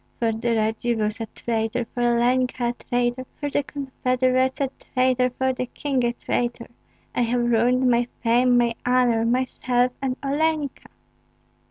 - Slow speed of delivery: No, average, 150 wpm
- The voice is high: Yes, high, 245 Hz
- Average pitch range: No, narrow, 1.4 semitones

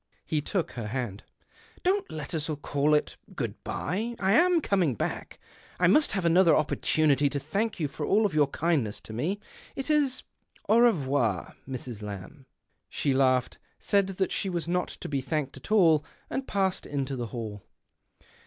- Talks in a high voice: No, medium, 155 Hz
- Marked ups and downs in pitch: Yes, wide, 6.6 semitones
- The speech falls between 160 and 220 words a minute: Yes, average, 170 wpm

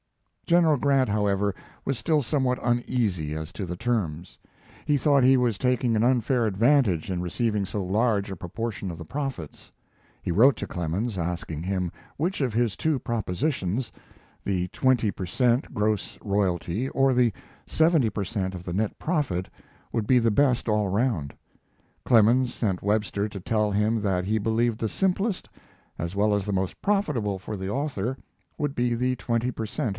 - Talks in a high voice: No, low, 110 Hz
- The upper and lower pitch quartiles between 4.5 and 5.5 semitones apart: Yes, average, 4.8 semitones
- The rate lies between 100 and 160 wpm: No, average, 170 wpm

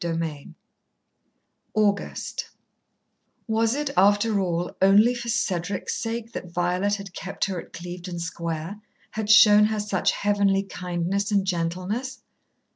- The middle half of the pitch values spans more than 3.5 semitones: No, average, 3.2 semitones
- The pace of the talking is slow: Yes, slow, 120 wpm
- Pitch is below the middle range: No, high, 195 Hz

